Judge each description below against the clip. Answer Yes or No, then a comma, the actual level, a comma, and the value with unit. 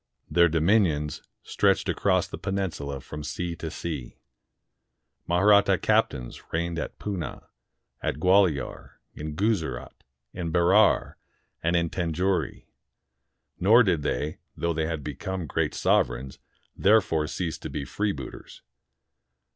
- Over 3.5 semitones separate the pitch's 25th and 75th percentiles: Yes, average, 4.1 semitones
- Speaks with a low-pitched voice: Yes, very low, 85 Hz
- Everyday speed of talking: No, slow, 115 wpm